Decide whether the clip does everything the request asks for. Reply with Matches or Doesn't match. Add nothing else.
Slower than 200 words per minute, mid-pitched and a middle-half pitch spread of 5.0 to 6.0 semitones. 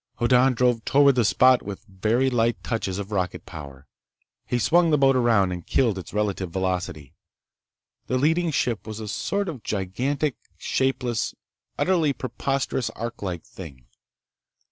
Doesn't match